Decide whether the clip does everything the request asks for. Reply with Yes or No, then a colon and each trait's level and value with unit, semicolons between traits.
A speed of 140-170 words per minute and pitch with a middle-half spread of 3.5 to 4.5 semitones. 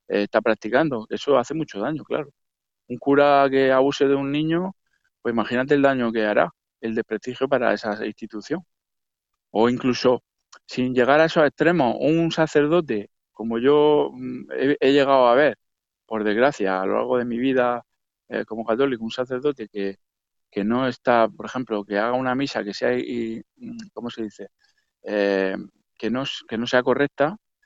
Yes: average, 165 wpm; average, 4.1 semitones